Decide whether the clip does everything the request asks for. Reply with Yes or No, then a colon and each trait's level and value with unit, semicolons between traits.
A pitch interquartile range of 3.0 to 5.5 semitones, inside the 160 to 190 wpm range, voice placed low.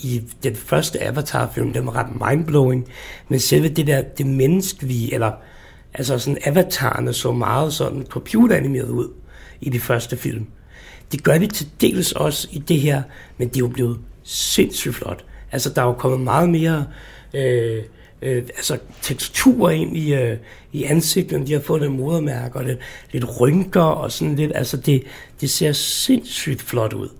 Yes: average, 3.6 semitones; average, 180 wpm; low, 130 Hz